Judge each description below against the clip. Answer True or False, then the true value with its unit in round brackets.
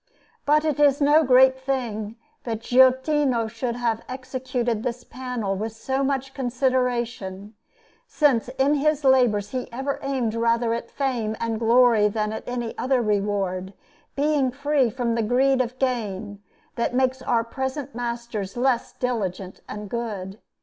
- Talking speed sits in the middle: True (145 wpm)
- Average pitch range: True (3.0 semitones)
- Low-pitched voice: False (245 Hz)